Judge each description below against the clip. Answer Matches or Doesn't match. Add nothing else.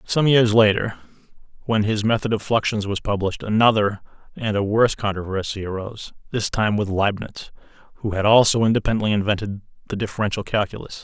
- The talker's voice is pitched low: Matches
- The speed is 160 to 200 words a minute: Doesn't match